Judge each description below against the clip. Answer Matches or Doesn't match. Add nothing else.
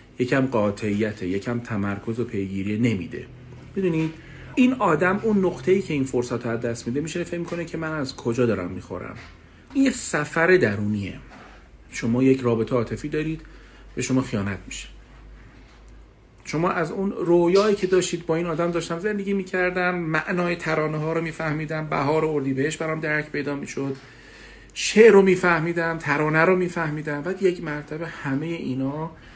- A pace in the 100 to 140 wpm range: Doesn't match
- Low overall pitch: Doesn't match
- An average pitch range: Doesn't match